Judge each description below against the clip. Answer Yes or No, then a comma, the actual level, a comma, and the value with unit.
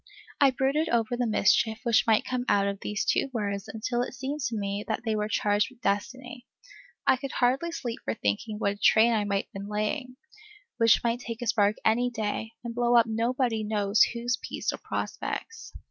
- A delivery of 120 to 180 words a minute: No, fast, 205 wpm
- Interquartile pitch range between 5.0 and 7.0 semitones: No, average, 2.9 semitones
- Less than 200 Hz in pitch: No, high, 230 Hz